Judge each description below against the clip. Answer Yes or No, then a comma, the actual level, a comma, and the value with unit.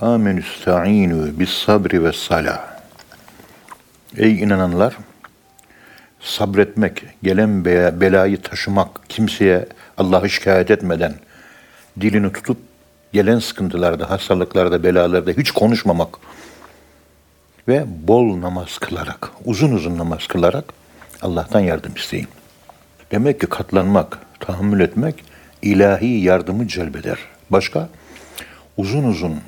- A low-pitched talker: Yes, very low, 95 Hz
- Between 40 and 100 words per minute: Yes, slow, 95 wpm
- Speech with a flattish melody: No, average, 3.3 semitones